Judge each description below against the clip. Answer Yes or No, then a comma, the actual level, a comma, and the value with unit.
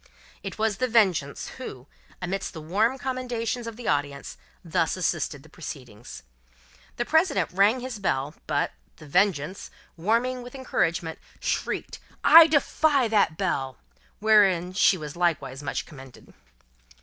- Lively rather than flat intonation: Yes, wide, 7.7 semitones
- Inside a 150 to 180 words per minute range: No, slow, 135 wpm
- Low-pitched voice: No, high, 190 Hz